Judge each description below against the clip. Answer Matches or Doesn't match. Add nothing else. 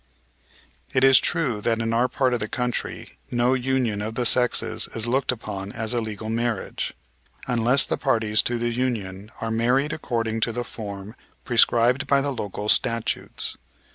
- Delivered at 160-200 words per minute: Matches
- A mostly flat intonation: Matches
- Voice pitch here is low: Matches